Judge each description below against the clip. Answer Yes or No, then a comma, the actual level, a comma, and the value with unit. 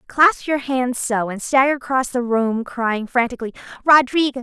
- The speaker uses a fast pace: No, average, 165 wpm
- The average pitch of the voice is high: Yes, very high, 255 Hz